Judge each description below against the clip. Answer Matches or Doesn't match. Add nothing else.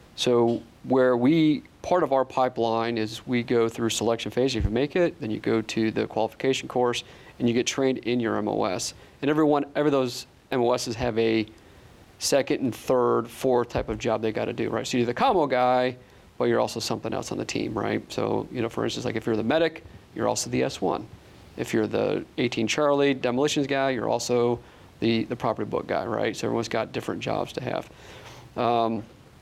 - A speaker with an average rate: Doesn't match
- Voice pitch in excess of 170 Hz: Doesn't match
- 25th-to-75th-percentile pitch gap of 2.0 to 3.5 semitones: Matches